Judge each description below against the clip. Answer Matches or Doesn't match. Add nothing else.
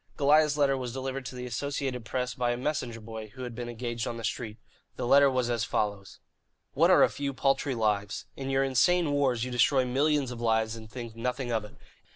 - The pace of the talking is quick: Matches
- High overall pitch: Doesn't match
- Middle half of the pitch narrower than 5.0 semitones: Matches